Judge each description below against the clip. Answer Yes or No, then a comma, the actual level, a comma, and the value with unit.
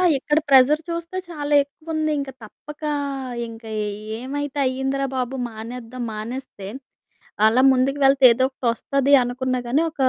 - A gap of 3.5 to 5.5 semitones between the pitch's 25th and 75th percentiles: No, average, 2.7 semitones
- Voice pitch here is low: No, very high, 265 Hz